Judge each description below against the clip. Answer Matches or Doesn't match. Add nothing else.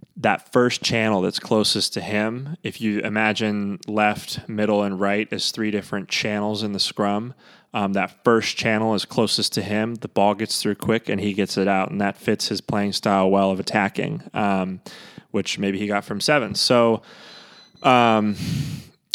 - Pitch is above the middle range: Doesn't match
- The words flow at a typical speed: Matches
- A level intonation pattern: Matches